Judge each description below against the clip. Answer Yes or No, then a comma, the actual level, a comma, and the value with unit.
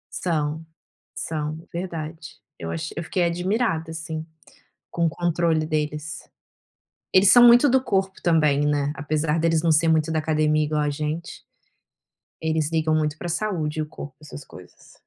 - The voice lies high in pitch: No, medium, 160 Hz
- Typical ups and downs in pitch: No, narrow, 2.0 semitones